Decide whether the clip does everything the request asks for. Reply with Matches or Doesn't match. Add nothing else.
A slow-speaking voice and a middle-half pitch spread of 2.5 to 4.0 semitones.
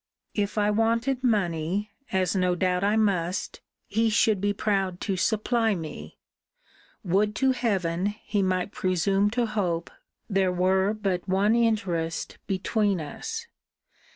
Matches